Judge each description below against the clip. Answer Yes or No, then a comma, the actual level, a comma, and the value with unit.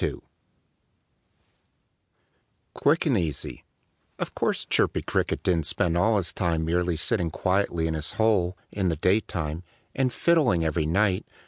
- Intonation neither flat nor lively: Yes, average, 4.3 semitones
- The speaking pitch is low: Yes, very low, 90 Hz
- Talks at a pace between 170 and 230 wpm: No, slow, 135 wpm